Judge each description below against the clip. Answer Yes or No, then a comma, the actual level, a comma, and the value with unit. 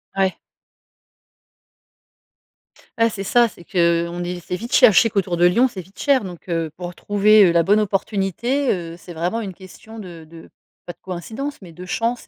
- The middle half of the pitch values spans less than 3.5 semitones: No, average, 4.0 semitones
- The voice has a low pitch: No, high, 190 Hz